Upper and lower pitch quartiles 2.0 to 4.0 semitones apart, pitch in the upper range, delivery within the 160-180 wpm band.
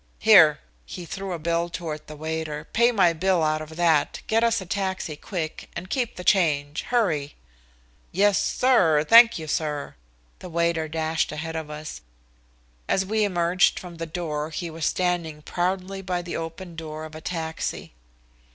No: average, 3.2 semitones; medium, 170 Hz; average, 170 wpm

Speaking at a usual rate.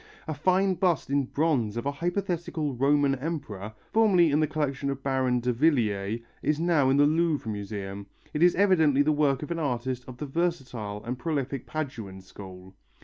Yes: average, 175 wpm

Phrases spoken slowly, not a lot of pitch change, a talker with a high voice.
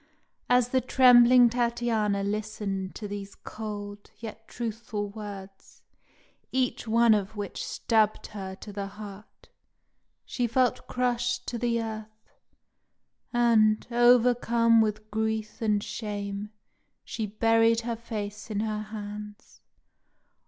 Yes: slow, 115 wpm; narrow, 2.3 semitones; high, 220 Hz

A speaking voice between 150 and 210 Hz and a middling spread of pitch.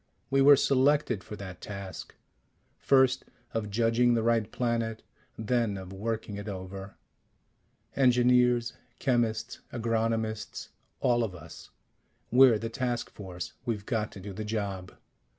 No: low, 115 Hz; average, 3.2 semitones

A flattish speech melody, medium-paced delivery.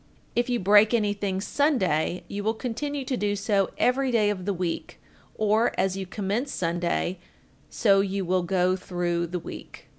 No: average, 3.6 semitones; average, 170 wpm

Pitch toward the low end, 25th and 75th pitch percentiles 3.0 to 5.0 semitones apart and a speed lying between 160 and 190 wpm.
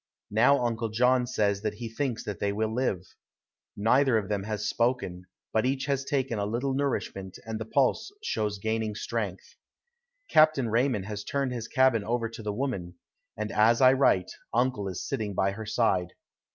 Yes: low, 110 Hz; average, 3.6 semitones; average, 180 wpm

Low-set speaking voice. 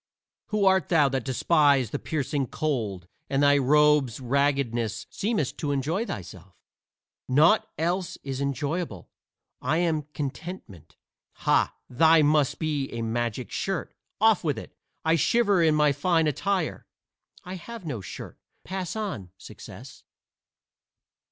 No: medium, 150 Hz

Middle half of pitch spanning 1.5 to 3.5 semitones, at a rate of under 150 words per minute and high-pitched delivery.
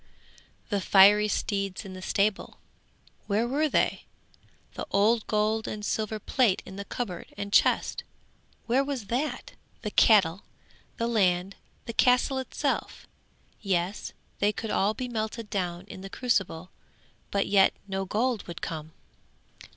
Yes: average, 3.1 semitones; slow, 135 wpm; high, 205 Hz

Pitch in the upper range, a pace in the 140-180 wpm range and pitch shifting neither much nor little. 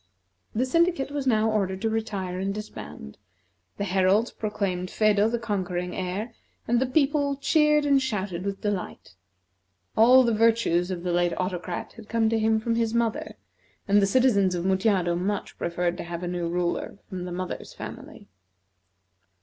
Yes: high, 205 Hz; average, 165 wpm; average, 4.2 semitones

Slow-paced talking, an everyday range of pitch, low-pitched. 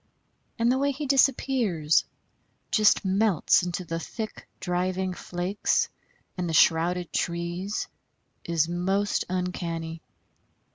No: slow, 105 wpm; average, 3.5 semitones; medium, 180 Hz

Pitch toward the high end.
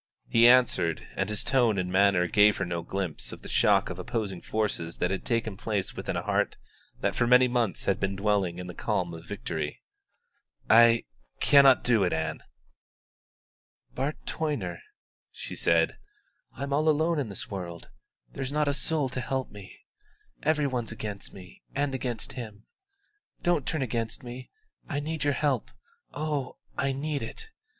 No: low, 115 Hz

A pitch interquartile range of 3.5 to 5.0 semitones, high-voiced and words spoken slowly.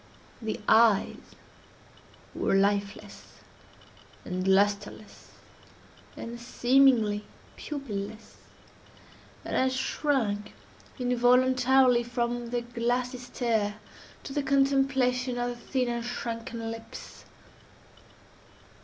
No: narrow, 2.6 semitones; high, 240 Hz; slow, 85 wpm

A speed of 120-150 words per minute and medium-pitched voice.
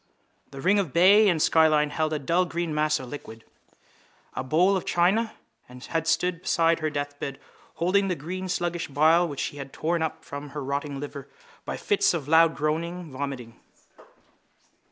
No: average, 175 wpm; medium, 160 Hz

